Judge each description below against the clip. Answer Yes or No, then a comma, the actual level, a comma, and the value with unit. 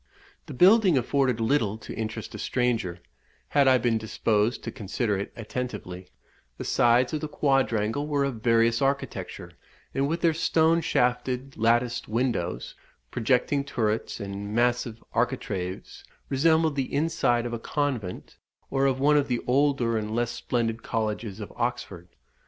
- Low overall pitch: Yes, low, 120 Hz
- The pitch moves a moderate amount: Yes, average, 3.7 semitones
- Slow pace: No, average, 145 wpm